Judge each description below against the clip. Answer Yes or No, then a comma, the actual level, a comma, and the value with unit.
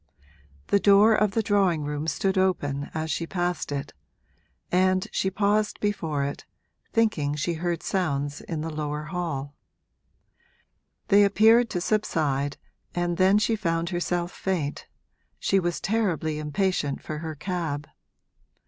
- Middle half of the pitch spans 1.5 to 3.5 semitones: No, average, 4.5 semitones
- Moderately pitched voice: Yes, medium, 175 Hz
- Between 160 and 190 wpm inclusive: No, slow, 135 wpm